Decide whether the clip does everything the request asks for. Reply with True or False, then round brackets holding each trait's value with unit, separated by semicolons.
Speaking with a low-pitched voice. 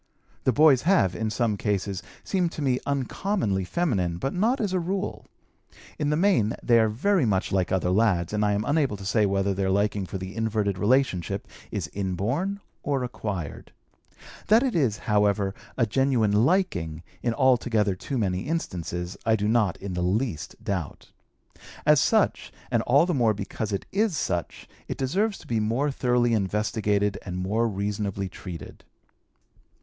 True (110 Hz)